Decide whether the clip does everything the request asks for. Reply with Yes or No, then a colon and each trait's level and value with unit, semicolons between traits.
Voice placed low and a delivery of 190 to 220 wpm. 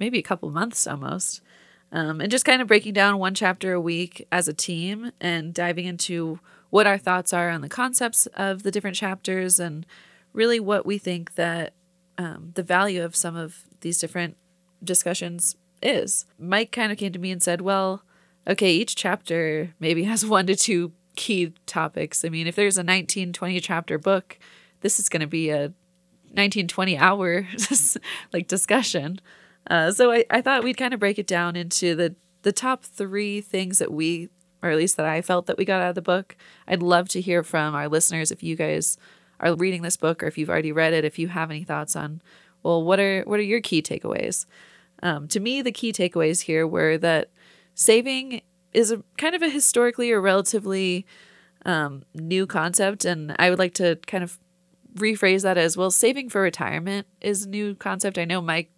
No: medium, 180 Hz; average, 200 wpm